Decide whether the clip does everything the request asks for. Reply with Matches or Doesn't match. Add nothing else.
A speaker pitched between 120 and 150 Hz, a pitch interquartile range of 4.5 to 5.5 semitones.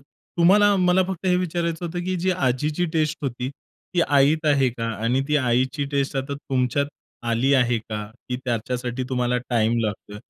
Matches